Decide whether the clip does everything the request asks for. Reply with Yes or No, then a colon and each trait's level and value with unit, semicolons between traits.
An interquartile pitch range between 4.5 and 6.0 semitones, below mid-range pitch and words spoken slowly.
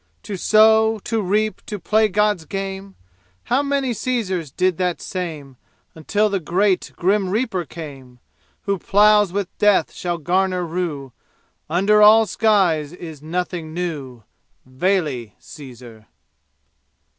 No: average, 4.8 semitones; medium, 185 Hz; slow, 125 wpm